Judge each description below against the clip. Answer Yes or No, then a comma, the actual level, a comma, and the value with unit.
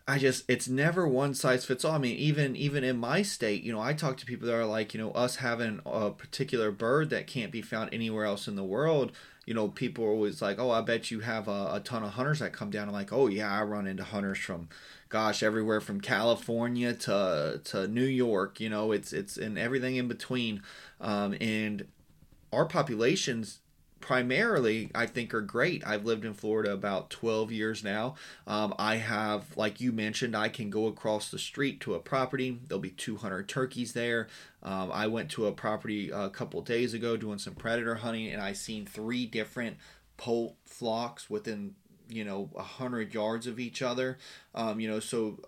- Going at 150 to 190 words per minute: No, fast, 205 wpm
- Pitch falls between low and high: No, low, 115 Hz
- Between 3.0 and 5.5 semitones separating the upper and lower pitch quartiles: No, narrow, 2.5 semitones